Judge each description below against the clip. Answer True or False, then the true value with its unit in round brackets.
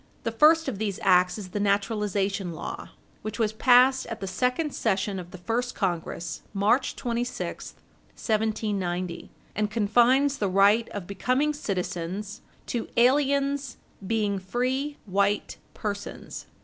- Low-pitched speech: False (210 Hz)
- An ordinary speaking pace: False (130 wpm)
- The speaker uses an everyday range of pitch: True (4.3 semitones)